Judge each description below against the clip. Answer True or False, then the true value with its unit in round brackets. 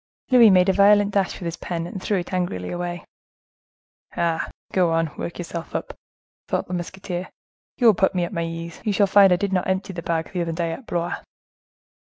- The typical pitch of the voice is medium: True (180 Hz)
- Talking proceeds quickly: True (210 wpm)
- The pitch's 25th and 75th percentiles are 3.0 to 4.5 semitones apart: False (2.4 semitones)